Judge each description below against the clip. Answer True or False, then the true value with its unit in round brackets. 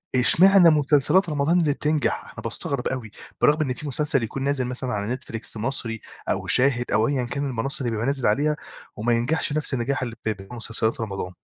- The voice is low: True (130 Hz)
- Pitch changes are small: False (4.2 semitones)